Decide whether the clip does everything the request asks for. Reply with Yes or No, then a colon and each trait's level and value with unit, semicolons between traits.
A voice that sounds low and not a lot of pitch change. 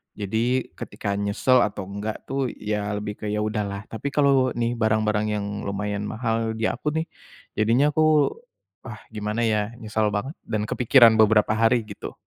Yes: low, 110 Hz; narrow, 2.3 semitones